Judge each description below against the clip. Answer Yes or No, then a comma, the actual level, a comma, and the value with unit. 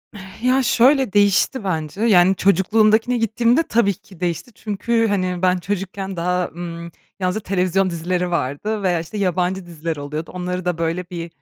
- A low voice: No, medium, 185 Hz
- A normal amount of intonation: Yes, average, 3.3 semitones